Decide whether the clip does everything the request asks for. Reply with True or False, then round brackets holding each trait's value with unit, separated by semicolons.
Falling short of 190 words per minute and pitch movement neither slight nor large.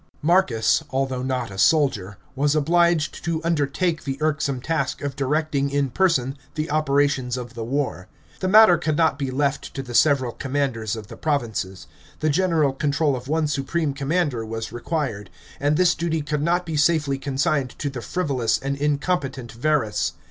True (175 wpm; 3.2 semitones)